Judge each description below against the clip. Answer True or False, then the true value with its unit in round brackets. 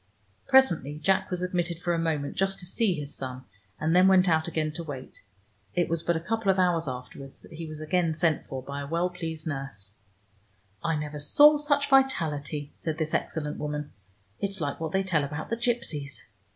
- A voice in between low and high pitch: True (160 Hz)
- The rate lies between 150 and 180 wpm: False (200 wpm)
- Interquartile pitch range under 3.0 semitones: False (3.6 semitones)